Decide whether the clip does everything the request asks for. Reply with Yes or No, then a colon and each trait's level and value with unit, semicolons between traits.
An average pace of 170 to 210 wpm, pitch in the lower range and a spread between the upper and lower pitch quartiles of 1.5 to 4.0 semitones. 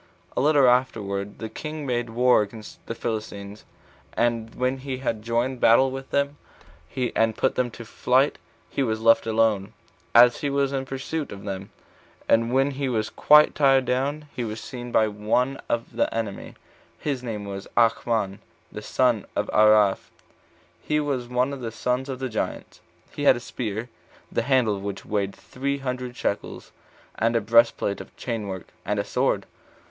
Yes: average, 175 wpm; low, 120 Hz; average, 3.4 semitones